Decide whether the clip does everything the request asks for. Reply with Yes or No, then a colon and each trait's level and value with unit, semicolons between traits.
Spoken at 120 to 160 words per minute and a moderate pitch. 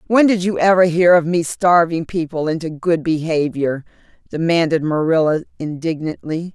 Yes: average, 140 wpm; medium, 165 Hz